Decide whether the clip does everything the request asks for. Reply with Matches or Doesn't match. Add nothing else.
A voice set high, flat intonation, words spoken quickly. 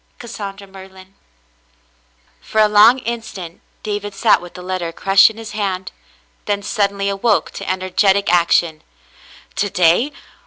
Doesn't match